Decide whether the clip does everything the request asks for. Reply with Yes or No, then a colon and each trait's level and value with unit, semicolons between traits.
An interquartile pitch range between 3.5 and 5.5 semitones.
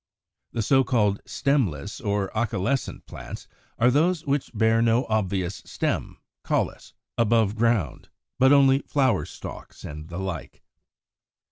Yes: average, 5.1 semitones